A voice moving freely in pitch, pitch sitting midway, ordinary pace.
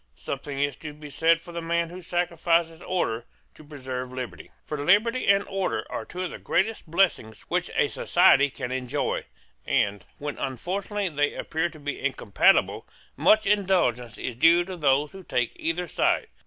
No: average, 5.0 semitones; medium, 160 Hz; average, 170 wpm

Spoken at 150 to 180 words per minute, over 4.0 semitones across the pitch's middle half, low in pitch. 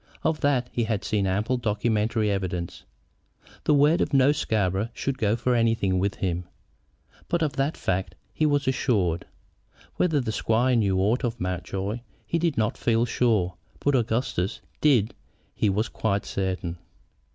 Yes: average, 160 wpm; average, 5.0 semitones; low, 110 Hz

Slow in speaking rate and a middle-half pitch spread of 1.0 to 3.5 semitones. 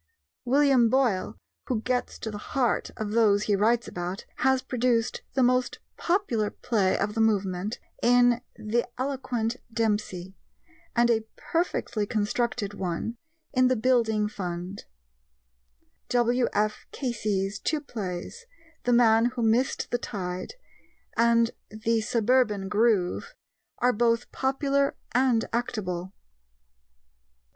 Yes: slow, 115 wpm; average, 3.1 semitones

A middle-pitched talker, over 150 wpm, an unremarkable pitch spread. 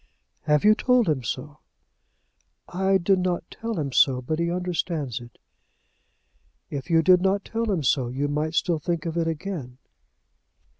Yes: medium, 165 Hz; average, 160 wpm; average, 4.3 semitones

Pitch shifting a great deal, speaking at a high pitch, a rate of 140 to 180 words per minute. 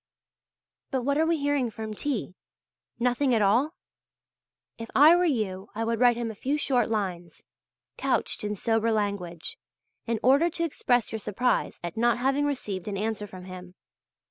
No: average, 4.7 semitones; high, 230 Hz; average, 170 wpm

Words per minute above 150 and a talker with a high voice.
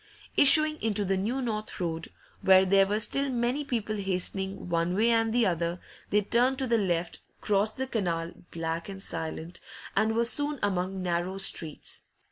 Yes: average, 170 wpm; high, 200 Hz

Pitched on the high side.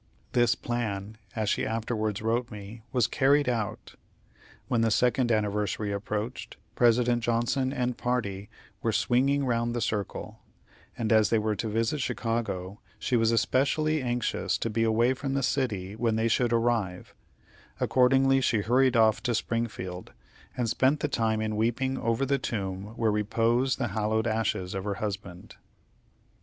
No: low, 115 Hz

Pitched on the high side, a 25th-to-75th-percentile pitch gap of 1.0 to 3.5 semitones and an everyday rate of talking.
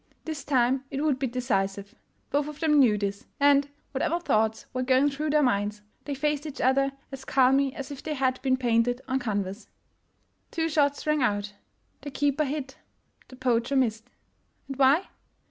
Yes: very high, 265 Hz; average, 3.1 semitones; average, 180 wpm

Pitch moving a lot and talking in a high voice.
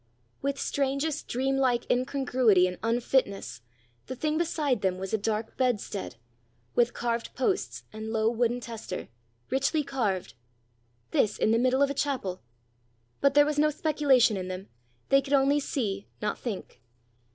No: average, 4.3 semitones; very high, 250 Hz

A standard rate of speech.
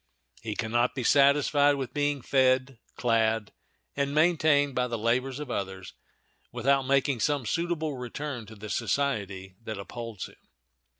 Yes: average, 145 wpm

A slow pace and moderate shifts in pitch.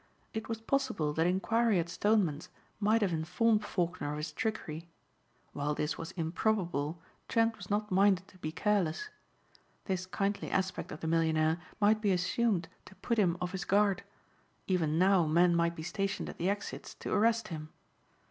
No: average, 170 wpm; average, 4.2 semitones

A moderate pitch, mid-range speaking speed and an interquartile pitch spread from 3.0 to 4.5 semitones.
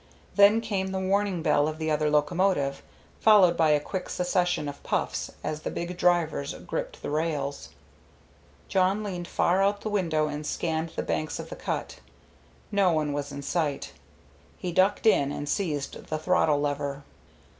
Yes: medium, 165 Hz; average, 165 wpm; average, 4.2 semitones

